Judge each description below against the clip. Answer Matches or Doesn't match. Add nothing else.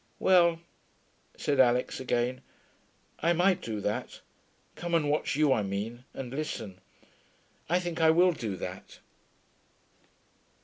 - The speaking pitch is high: Doesn't match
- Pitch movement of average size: Doesn't match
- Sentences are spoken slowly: Matches